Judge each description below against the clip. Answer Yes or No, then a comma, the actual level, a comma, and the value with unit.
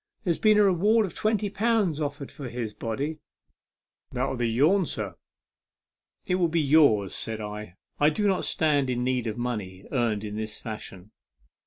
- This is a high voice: No, low, 135 Hz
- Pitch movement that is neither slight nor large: No, wide, 7.9 semitones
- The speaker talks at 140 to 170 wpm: No, average, 180 wpm